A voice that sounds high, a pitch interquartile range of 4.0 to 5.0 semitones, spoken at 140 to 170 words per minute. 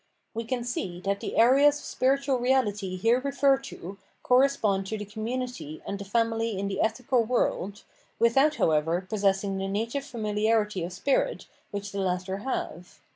Yes: high, 220 Hz; average, 4.4 semitones; average, 165 wpm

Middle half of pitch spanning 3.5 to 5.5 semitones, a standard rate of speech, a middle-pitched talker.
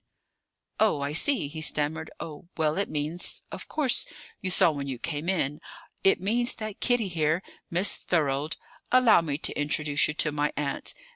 Yes: average, 4.6 semitones; average, 170 wpm; medium, 160 Hz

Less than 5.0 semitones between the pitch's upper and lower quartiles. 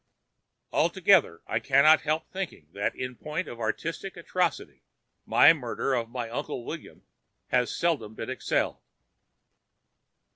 No: wide, 5.6 semitones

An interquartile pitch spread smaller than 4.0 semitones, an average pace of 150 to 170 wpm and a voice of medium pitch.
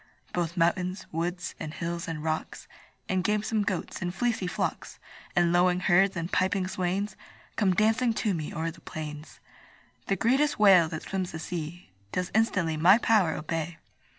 Yes: average, 3.1 semitones; average, 160 wpm; medium, 180 Hz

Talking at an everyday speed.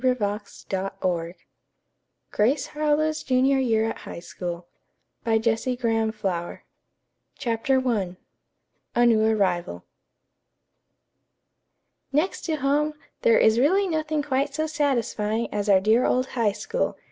No: slow, 105 wpm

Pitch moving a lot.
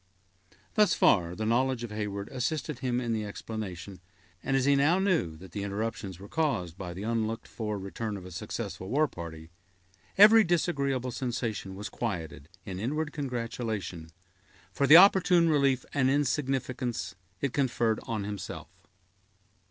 Yes: wide, 5.7 semitones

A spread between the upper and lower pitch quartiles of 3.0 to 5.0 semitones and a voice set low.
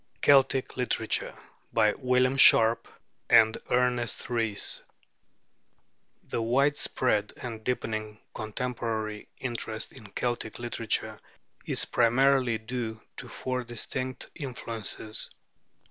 No: narrow, 2.4 semitones; low, 120 Hz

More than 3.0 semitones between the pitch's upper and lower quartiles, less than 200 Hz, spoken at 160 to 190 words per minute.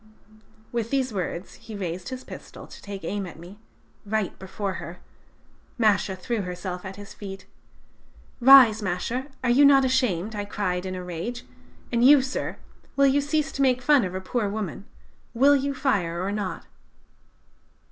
No: wide, 5.6 semitones; high, 210 Hz; average, 165 wpm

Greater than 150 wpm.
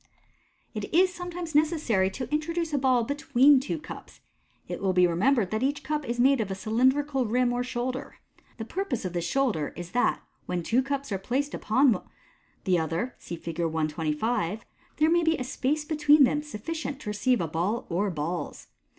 Yes: average, 190 wpm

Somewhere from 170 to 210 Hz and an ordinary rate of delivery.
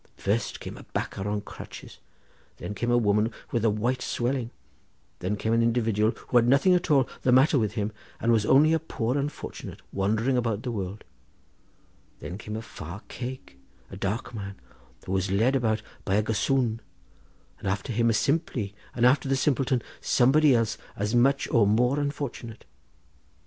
No: low, 115 Hz; average, 170 wpm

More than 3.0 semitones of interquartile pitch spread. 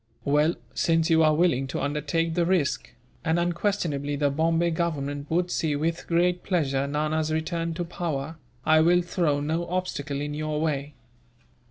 No: average, 2.7 semitones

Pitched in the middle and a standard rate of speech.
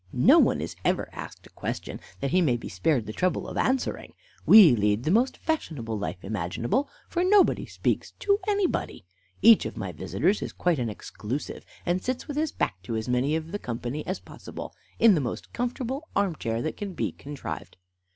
Yes: medium, 155 Hz; average, 195 wpm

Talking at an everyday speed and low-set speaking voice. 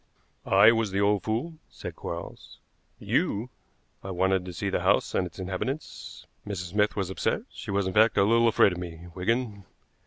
Yes: average, 185 wpm; low, 100 Hz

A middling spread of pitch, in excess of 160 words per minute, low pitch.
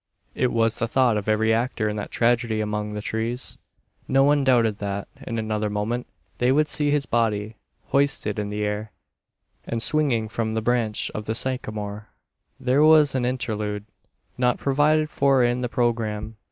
Yes: average, 3.3 semitones; average, 170 wpm; low, 115 Hz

